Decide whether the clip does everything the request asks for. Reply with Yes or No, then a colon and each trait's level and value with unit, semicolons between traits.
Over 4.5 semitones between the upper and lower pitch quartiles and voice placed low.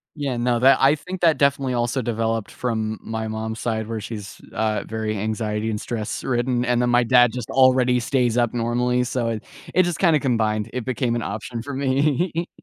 No: average, 2.8 semitones; low, 120 Hz